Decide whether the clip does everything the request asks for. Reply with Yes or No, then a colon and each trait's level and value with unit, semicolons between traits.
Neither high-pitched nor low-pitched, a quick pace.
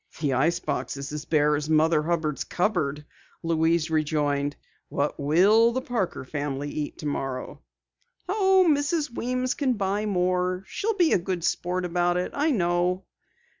No: medium, 175 Hz; average, 150 wpm